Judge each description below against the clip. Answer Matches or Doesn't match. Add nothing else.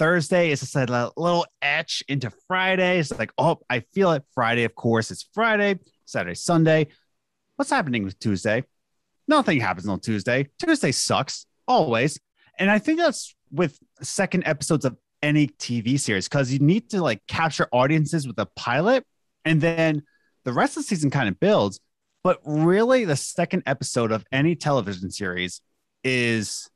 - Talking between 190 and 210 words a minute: Doesn't match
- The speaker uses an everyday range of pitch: Doesn't match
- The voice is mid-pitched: Matches